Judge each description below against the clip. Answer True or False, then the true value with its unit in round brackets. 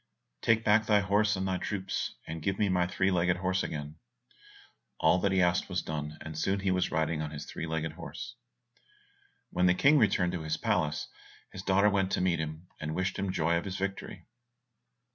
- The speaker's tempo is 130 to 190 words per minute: False (200 wpm)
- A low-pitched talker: True (90 Hz)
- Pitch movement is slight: False (3.4 semitones)